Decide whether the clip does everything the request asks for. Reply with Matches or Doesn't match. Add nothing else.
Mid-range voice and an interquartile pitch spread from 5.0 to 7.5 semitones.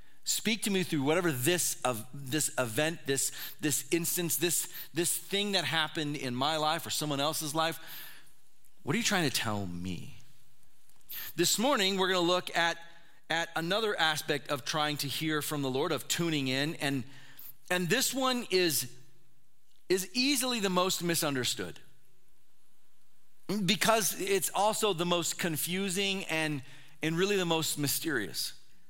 Doesn't match